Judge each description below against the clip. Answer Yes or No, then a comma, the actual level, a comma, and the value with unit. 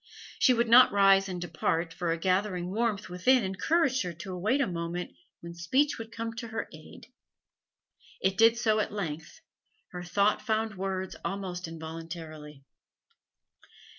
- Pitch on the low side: No, high, 190 Hz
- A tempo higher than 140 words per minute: Yes, average, 150 wpm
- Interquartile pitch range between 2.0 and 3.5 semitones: No, average, 4.7 semitones